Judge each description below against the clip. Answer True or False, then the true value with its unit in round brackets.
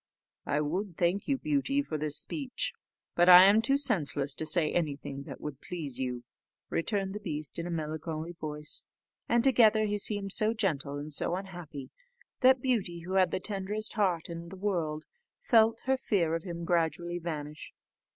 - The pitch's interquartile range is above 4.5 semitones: True (5.3 semitones)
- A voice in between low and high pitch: True (175 Hz)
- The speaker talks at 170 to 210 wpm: True (175 wpm)